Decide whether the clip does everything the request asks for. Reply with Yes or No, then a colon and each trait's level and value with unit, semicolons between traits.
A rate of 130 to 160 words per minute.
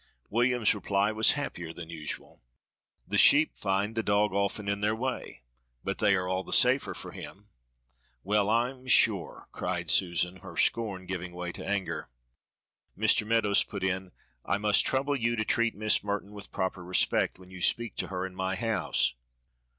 No: average, 175 wpm